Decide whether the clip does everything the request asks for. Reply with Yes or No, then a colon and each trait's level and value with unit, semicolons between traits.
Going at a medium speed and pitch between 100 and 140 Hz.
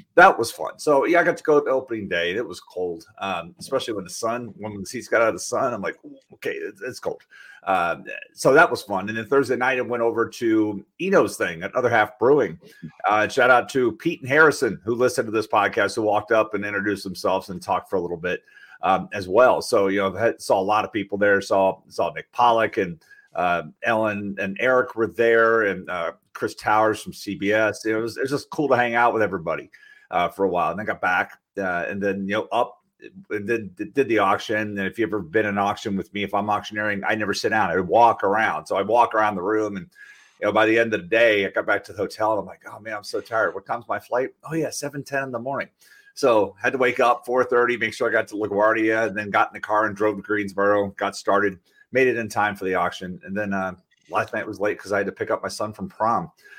No: fast, 265 wpm; low, 110 Hz